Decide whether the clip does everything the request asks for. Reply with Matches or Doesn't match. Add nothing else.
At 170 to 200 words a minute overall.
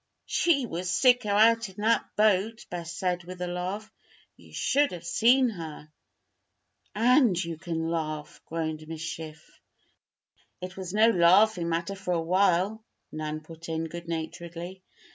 Doesn't match